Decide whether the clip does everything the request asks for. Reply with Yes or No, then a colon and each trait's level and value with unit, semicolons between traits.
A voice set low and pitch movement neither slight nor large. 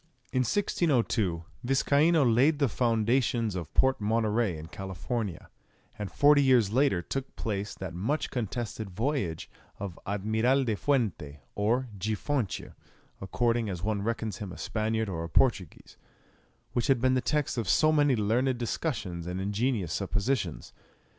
Yes: low, 110 Hz; average, 5.0 semitones